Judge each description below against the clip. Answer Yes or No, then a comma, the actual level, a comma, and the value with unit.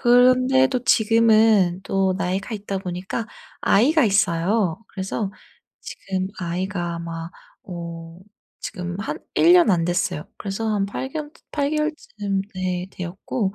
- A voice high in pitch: Yes, high, 195 Hz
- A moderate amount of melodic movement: Yes, average, 4.3 semitones